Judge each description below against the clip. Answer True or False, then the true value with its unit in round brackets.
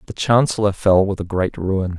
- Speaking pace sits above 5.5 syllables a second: False (5.0 syllables/s)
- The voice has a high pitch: False (95 Hz)